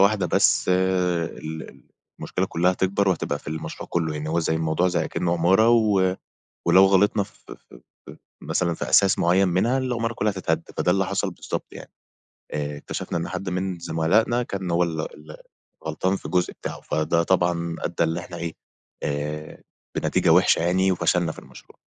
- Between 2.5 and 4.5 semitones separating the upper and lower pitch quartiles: Yes, average, 2.8 semitones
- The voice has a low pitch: Yes, very low, 90 Hz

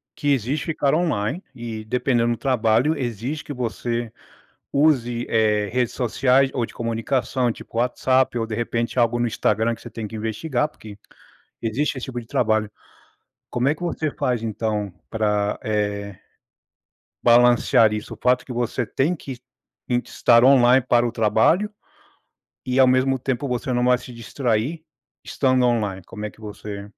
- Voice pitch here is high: No, low, 120 Hz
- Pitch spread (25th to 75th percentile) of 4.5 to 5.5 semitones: No, average, 2.9 semitones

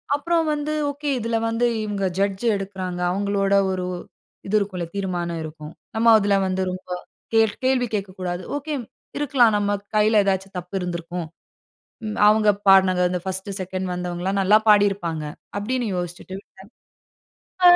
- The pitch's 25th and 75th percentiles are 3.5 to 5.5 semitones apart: No, average, 2.8 semitones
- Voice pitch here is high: Yes, high, 195 Hz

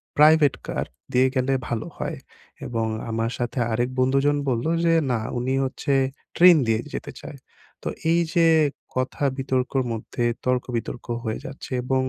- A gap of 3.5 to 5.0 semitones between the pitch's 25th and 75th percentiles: No, narrow, 2.5 semitones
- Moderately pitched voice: No, low, 130 Hz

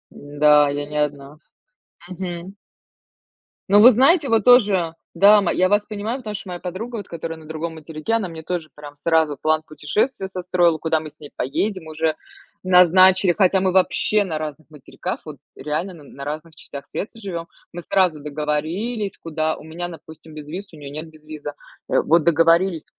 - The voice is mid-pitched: Yes, medium, 165 Hz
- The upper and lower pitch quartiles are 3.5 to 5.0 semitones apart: Yes, average, 3.8 semitones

